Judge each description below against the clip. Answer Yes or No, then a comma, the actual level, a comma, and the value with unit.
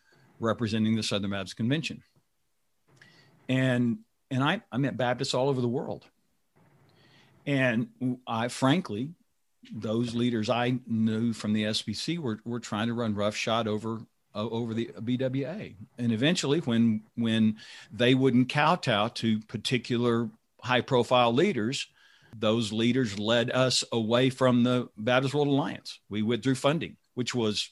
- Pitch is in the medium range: No, low, 120 Hz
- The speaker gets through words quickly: No, slow, 135 wpm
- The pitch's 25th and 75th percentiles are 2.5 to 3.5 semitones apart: Yes, average, 2.8 semitones